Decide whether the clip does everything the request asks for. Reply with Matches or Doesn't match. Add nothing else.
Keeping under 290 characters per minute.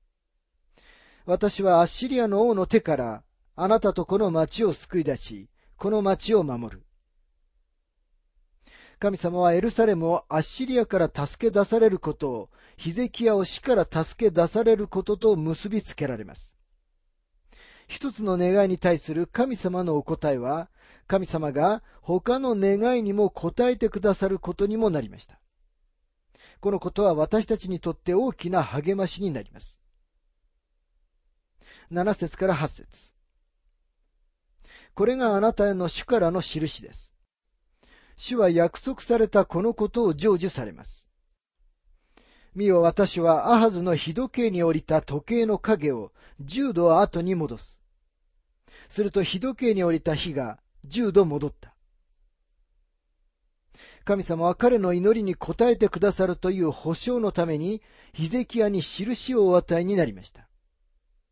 Matches